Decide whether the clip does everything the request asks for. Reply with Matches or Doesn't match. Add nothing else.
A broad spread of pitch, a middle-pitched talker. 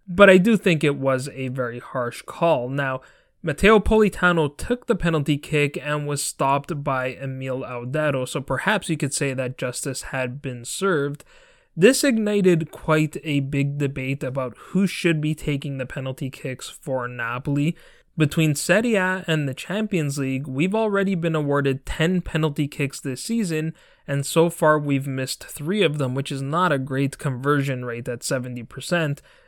Doesn't match